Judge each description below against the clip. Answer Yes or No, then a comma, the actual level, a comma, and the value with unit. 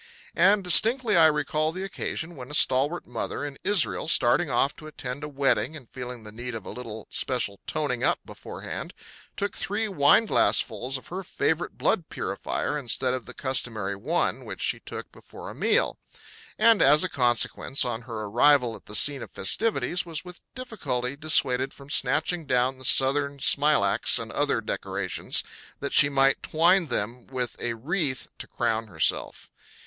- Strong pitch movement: No, average, 4.8 semitones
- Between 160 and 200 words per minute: Yes, average, 170 wpm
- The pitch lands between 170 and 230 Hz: No, medium, 140 Hz